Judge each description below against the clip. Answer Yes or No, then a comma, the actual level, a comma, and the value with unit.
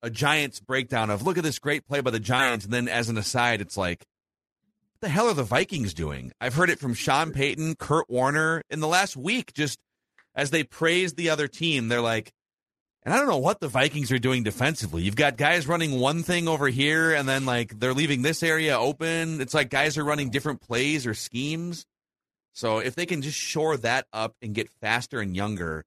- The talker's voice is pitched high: No, low, 135 Hz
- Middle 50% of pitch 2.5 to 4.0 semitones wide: No, average, 4.9 semitones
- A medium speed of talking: No, fast, 220 wpm